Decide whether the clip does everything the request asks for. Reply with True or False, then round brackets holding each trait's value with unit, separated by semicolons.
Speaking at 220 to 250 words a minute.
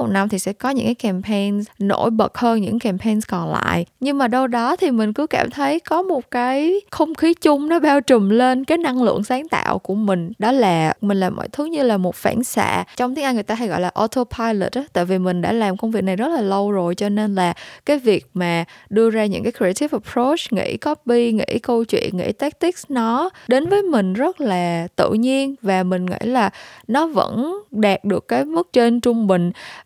True (230 wpm)